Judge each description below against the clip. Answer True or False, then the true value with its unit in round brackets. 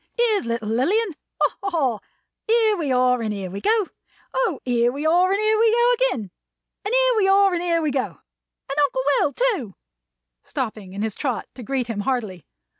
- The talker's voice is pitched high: True (290 Hz)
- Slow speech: False (195 wpm)